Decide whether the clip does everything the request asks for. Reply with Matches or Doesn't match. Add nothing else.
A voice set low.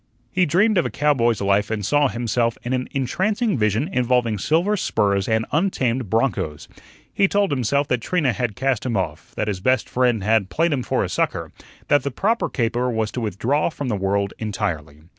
Matches